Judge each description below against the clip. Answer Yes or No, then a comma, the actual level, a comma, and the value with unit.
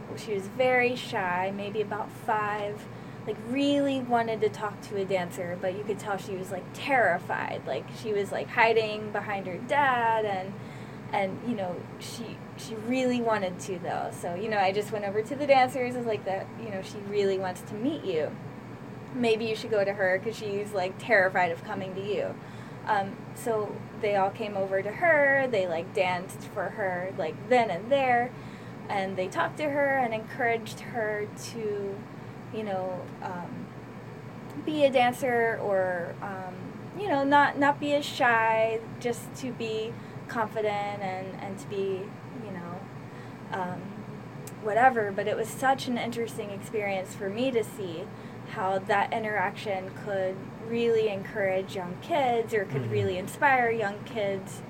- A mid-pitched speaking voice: No, high, 210 Hz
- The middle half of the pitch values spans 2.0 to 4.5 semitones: Yes, average, 3.4 semitones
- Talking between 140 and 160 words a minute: No, average, 170 wpm